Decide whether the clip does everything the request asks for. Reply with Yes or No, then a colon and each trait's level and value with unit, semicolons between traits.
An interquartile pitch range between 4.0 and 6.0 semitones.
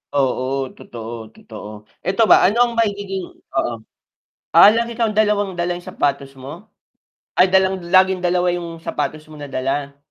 Yes: wide, 5.6 semitones